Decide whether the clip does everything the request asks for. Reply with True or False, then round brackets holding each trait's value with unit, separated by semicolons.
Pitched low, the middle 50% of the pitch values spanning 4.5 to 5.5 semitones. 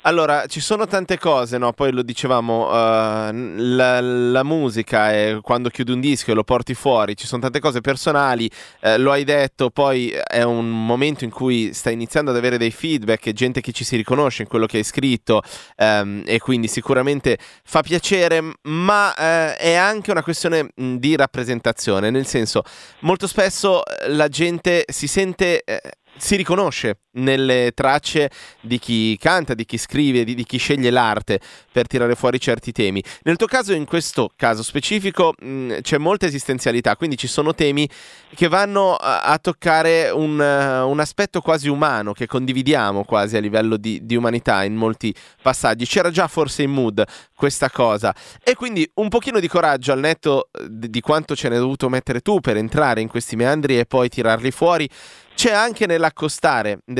True (130 Hz; 5.0 semitones)